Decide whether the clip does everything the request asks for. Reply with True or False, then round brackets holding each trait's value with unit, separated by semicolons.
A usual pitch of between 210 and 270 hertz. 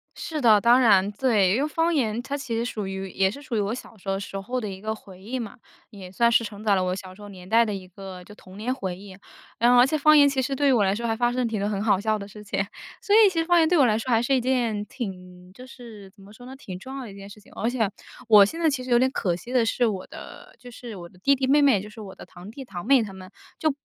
True (220 Hz)